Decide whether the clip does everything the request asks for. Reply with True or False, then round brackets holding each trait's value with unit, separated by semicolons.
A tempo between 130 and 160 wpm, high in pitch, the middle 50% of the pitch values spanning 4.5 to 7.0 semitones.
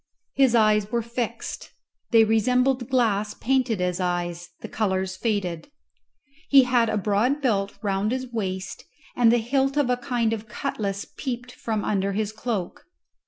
False (155 wpm; 220 Hz; 3.8 semitones)